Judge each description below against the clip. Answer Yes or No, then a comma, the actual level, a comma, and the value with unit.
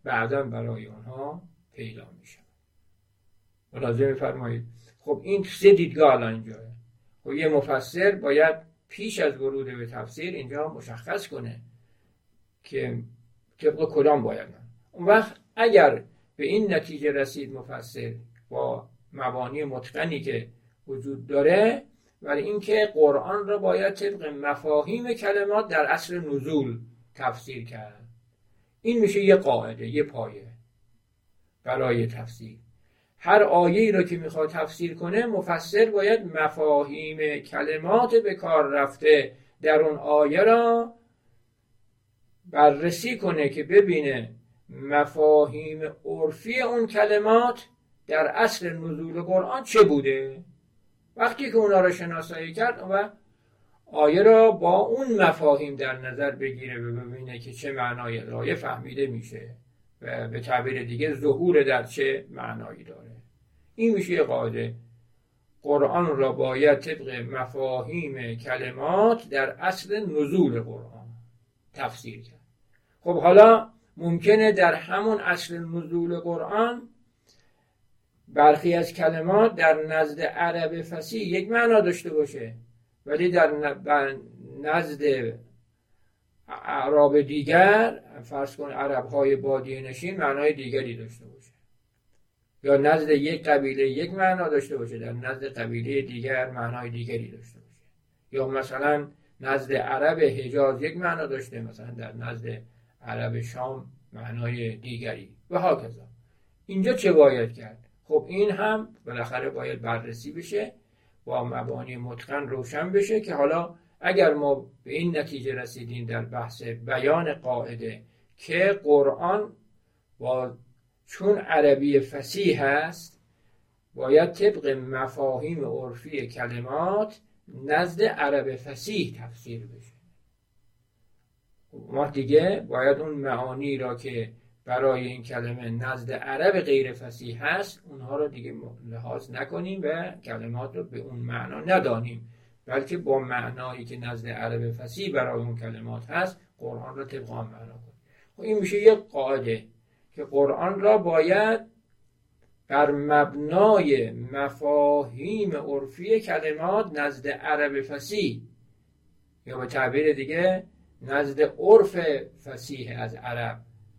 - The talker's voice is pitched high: No, medium, 140 Hz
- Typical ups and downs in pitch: No, wide, 6.2 semitones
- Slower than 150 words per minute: Yes, average, 120 wpm